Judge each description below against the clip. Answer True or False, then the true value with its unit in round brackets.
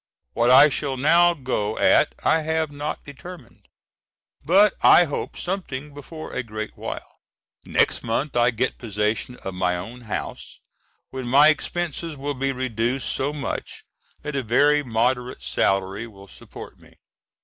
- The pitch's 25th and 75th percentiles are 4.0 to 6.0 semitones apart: True (4.5 semitones)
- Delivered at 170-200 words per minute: False (150 wpm)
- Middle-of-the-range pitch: False (130 Hz)